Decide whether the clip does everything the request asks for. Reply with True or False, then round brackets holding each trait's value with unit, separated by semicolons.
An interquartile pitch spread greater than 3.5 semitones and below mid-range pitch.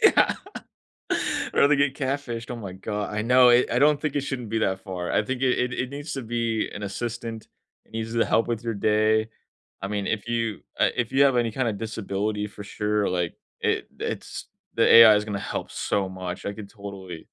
False (3.1 semitones; 110 Hz)